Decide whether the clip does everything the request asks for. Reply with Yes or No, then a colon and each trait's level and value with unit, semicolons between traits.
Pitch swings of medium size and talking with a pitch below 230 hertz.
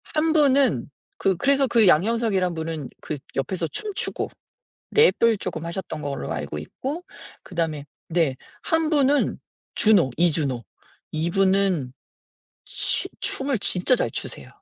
No: wide, 9.0 semitones; high, 190 Hz